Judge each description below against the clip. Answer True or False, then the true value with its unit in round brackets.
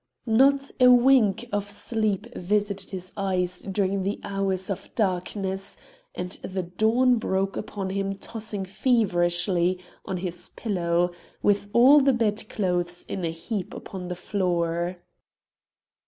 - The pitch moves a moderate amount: True (3.0 semitones)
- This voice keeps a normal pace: False (125 wpm)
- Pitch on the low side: False (195 Hz)